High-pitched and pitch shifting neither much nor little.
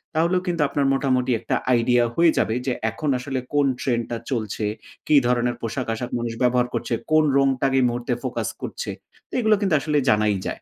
No: low, 125 Hz; average, 3.3 semitones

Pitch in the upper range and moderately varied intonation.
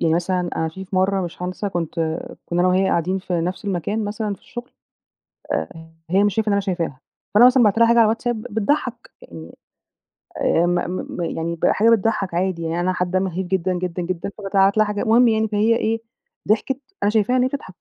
Yes: high, 195 Hz; average, 3.7 semitones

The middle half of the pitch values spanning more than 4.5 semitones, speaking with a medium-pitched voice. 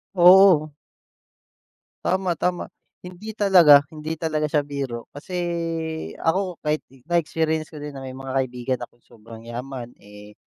Yes: average, 4.9 semitones; medium, 150 Hz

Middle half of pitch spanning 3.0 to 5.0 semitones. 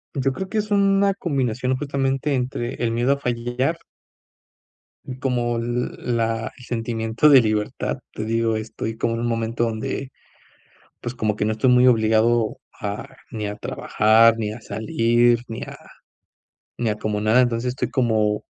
No: narrow, 2.5 semitones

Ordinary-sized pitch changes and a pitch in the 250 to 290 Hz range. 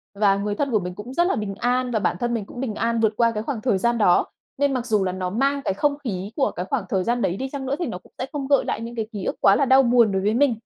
No: average, 4.5 semitones; high, 230 Hz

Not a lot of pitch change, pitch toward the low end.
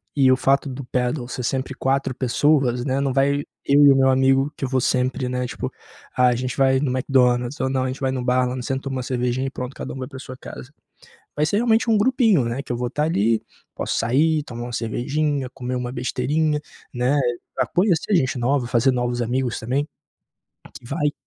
Yes: narrow, 2.2 semitones; low, 130 Hz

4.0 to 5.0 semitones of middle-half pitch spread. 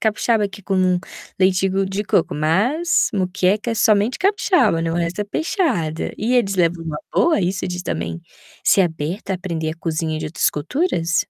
Yes: average, 4.3 semitones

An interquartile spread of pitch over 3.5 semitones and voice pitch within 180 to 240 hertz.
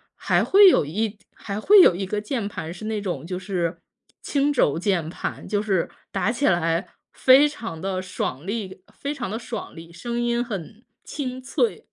Yes: average, 5.3 semitones; high, 205 Hz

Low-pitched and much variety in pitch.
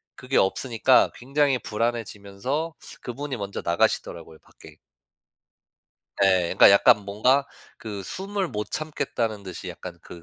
Yes: low, 115 Hz; wide, 5.7 semitones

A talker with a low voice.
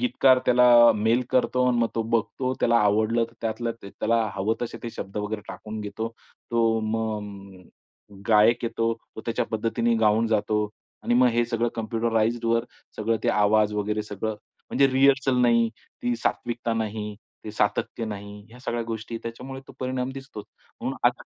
Yes: low, 115 Hz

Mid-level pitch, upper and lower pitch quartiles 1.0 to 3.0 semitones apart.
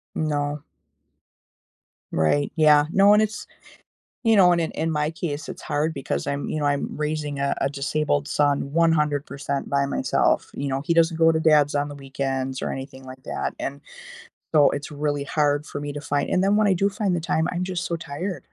Yes: medium, 150 Hz; narrow, 2.5 semitones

